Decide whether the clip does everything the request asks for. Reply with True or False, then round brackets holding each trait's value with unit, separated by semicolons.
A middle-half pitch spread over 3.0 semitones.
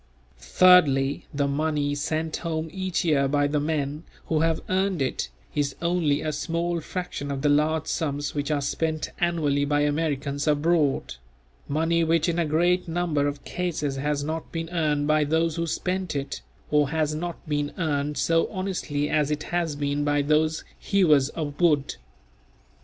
False (2.5 semitones)